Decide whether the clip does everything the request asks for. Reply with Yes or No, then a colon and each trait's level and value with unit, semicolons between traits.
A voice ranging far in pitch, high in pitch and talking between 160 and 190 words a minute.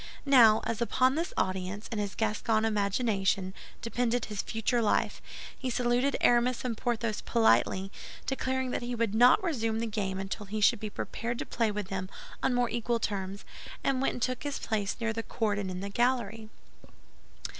No: average, 3.0 semitones; high, 225 Hz; average, 180 wpm